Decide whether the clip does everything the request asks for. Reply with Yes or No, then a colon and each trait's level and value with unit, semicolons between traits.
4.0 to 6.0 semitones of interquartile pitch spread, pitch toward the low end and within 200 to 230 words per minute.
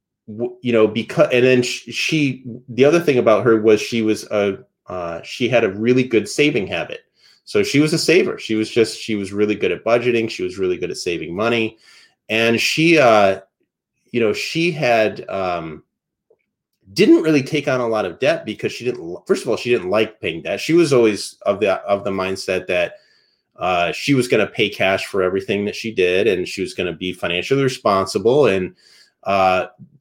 Yes: average, 5.3 semitones; low, 115 Hz; fast, 205 wpm